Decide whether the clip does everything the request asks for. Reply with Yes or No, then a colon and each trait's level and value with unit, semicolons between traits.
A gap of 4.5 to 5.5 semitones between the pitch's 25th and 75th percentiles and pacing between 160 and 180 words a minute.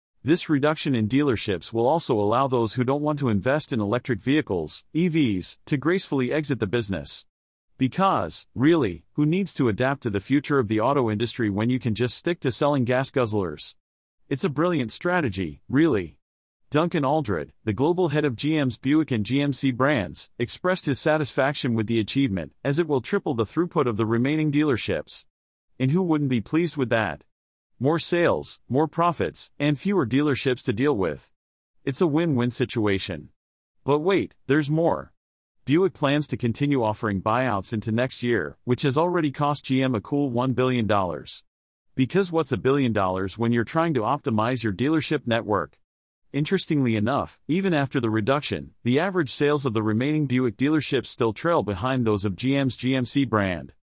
Yes: average, 4.9 semitones; average, 170 wpm